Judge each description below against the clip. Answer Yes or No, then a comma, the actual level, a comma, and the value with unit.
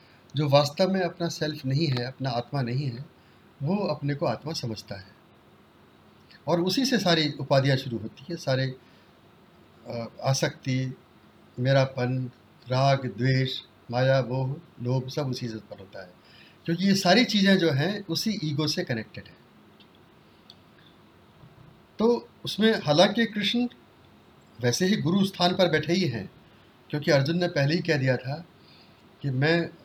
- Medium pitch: Yes, medium, 145 Hz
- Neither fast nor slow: Yes, average, 145 wpm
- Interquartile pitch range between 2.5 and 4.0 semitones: No, average, 5.3 semitones